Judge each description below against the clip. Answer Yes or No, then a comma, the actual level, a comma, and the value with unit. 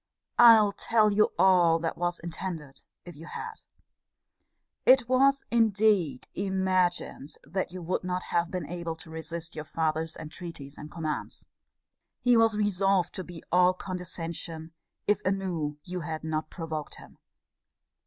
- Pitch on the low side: No, medium, 175 Hz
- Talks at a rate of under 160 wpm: Yes, average, 140 wpm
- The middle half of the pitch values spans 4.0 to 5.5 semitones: No, average, 3.3 semitones